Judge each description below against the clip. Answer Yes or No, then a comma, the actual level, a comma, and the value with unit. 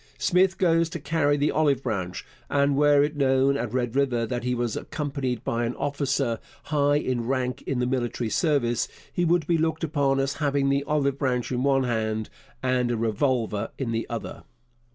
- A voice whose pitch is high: No, low, 135 Hz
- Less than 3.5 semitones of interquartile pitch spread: Yes, average, 3.1 semitones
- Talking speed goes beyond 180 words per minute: Yes, average, 190 wpm